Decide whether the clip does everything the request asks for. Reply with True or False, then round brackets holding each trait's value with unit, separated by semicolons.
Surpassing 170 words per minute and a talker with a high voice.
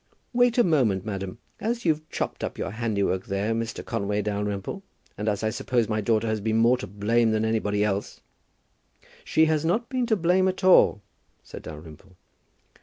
False (180 wpm; 110 Hz)